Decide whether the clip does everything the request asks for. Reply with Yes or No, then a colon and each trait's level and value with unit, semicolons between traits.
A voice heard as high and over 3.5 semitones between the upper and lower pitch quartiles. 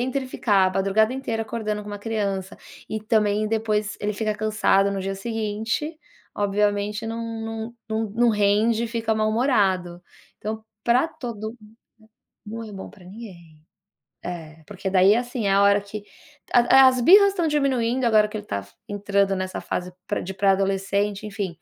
No: high, 210 Hz; narrow, 2.4 semitones